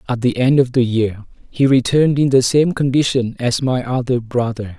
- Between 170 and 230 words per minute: Yes, average, 200 wpm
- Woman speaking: No, male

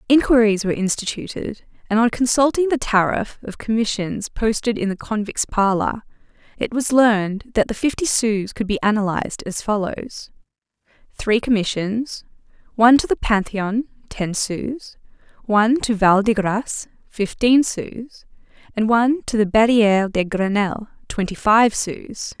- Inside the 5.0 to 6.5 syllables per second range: No, 4.6 syllables/s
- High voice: Yes, high, 220 Hz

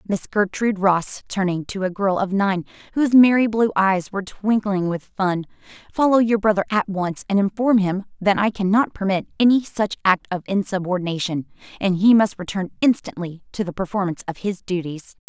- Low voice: No, high, 195 Hz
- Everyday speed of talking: Yes, average, 175 wpm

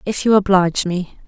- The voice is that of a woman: Yes, female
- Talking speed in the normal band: Yes, average, 190 wpm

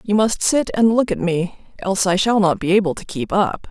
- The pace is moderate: No, fast, 260 wpm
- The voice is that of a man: No, female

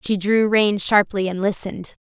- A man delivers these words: No, female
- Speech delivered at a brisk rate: No, average, 180 wpm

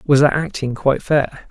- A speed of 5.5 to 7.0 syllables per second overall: No, 5.0 syllables/s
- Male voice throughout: Yes, male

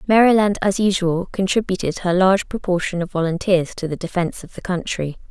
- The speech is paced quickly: No, average, 170 wpm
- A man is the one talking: No, female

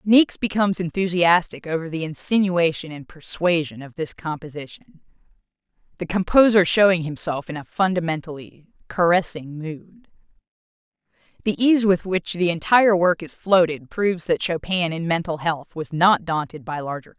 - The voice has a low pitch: No, medium, 170 Hz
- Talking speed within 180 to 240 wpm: No, average, 145 wpm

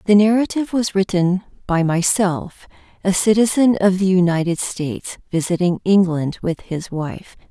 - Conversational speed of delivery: No, slow, 130 wpm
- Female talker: Yes, female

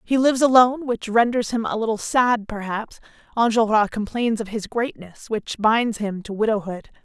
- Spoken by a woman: Yes, female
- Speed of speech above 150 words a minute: Yes, average, 170 wpm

